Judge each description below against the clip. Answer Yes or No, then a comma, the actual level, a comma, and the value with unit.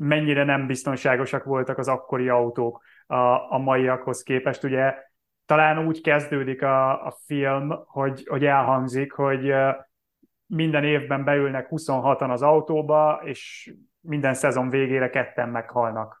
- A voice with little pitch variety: Yes, narrow, 1.8 semitones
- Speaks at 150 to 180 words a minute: No, average, 120 wpm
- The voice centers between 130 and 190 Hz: Yes, low, 135 Hz